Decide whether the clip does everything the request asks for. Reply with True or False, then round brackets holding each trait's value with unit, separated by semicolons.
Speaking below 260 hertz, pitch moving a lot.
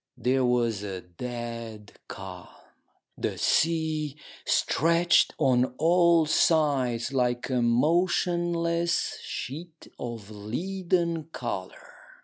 True (135 Hz; 6.1 semitones)